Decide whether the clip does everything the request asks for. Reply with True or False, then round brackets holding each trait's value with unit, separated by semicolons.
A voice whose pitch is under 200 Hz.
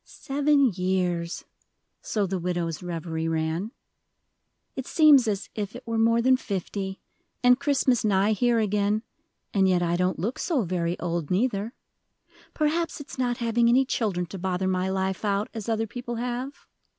False (205 Hz)